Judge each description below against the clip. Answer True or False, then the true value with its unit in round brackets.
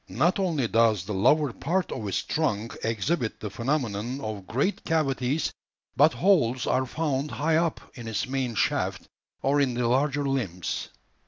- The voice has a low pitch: True (130 Hz)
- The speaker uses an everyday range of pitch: True (4.9 semitones)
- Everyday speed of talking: True (160 wpm)